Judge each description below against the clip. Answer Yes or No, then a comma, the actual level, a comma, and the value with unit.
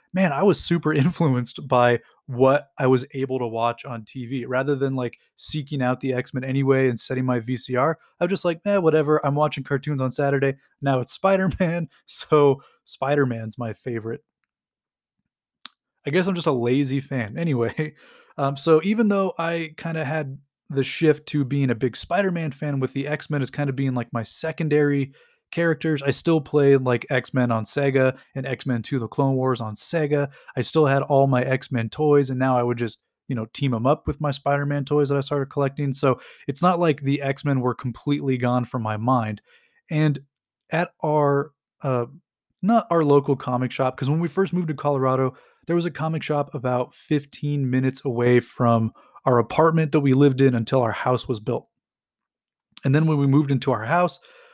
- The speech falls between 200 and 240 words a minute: Yes, fast, 205 wpm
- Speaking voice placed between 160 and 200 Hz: No, medium, 140 Hz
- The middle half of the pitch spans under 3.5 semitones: Yes, average, 3.1 semitones